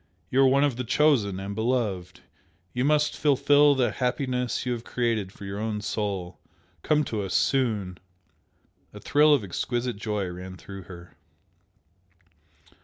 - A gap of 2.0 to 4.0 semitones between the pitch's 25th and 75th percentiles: No, average, 5.1 semitones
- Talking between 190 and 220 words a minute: No, average, 150 wpm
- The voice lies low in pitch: Yes, low, 115 Hz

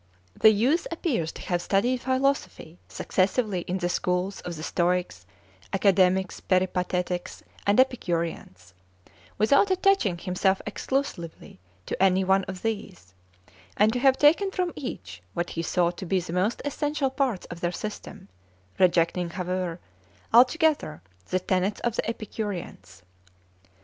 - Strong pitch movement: Yes, wide, 5.8 semitones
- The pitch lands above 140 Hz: Yes, high, 190 Hz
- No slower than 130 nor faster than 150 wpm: Yes, slow, 135 wpm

